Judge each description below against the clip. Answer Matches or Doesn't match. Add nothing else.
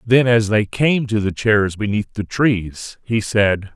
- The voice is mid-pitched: Doesn't match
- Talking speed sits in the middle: Matches